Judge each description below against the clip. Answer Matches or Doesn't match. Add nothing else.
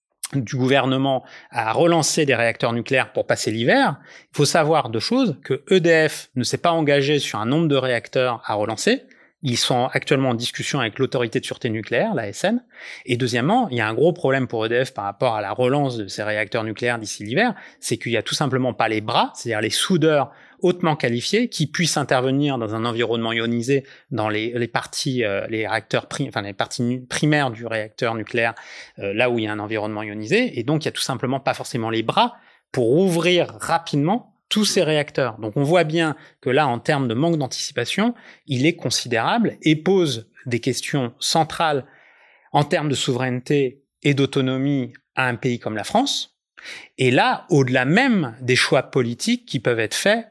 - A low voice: Matches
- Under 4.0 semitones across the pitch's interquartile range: Doesn't match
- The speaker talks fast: Doesn't match